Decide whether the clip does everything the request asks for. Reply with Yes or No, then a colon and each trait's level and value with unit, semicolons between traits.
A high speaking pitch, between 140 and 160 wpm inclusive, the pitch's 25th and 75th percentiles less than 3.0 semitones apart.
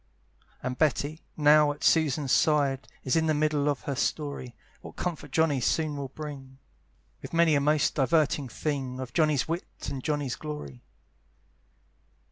No: medium, 145 Hz; average, 150 wpm; narrow, 2.4 semitones